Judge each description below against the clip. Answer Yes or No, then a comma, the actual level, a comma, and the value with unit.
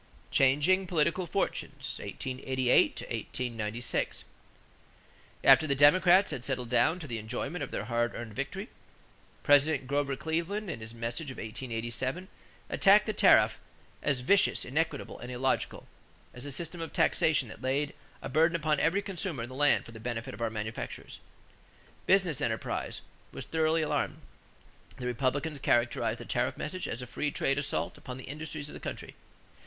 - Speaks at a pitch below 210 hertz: Yes, medium, 140 Hz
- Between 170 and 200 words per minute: No, average, 155 wpm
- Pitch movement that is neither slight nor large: Yes, average, 4.7 semitones